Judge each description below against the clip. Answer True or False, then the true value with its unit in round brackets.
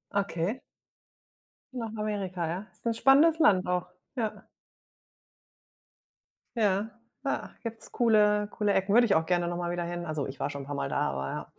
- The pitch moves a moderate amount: True (4.3 semitones)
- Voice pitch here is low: False (195 Hz)